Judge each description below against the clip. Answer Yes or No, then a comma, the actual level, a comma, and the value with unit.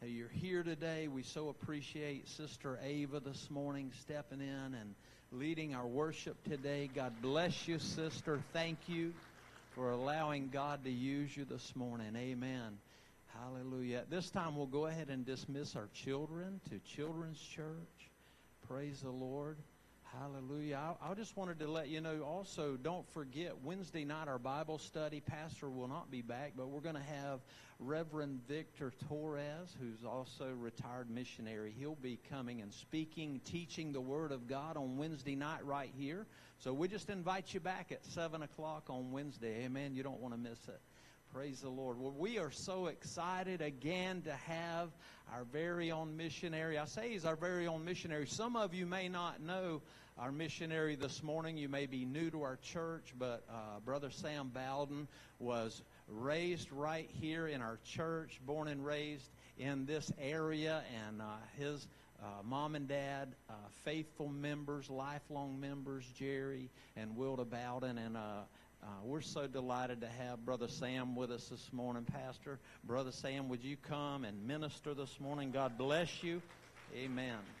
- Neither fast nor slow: Yes, average, 170 wpm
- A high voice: No, medium, 145 Hz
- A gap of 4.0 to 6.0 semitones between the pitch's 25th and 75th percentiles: No, average, 3.5 semitones